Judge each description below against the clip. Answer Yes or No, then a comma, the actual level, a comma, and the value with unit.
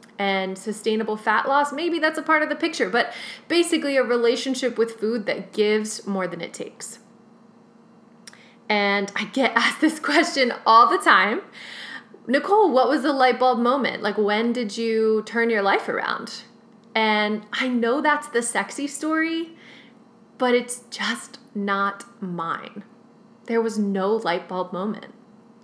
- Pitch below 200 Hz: No, high, 230 Hz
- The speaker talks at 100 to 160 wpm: Yes, average, 150 wpm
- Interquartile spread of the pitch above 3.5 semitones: No, average, 3.2 semitones